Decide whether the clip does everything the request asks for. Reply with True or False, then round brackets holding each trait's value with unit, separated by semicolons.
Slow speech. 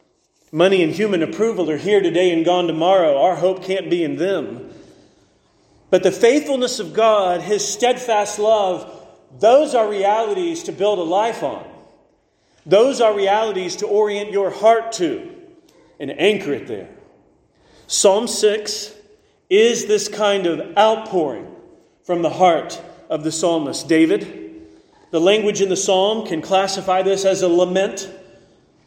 False (145 wpm)